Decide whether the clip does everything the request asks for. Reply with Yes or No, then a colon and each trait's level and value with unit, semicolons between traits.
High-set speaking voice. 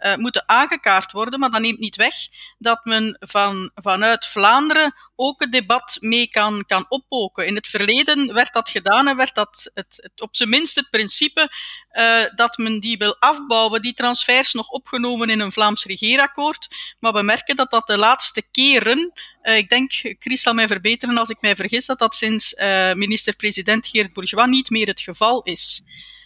Yes: high, 230 Hz